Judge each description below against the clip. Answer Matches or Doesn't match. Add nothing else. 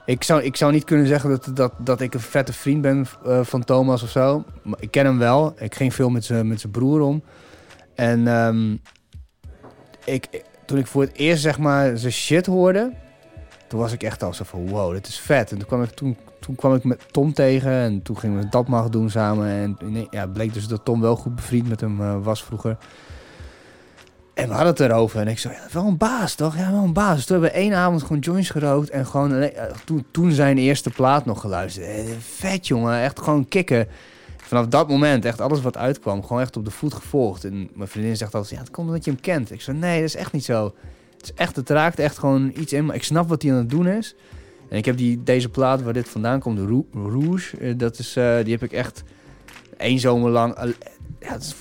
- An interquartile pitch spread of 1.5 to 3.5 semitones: Doesn't match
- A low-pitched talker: Matches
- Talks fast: Matches